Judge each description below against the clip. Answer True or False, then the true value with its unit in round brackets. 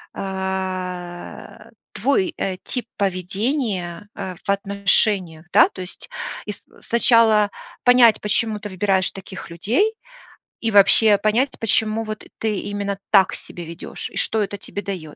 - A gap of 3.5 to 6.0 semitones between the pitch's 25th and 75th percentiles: False (2.7 semitones)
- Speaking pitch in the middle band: False (200 Hz)